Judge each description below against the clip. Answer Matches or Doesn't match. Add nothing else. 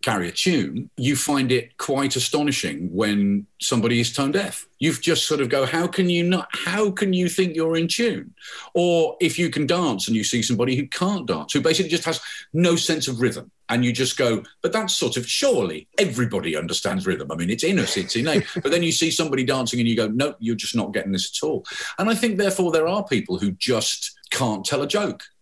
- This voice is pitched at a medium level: Matches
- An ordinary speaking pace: Doesn't match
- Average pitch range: Doesn't match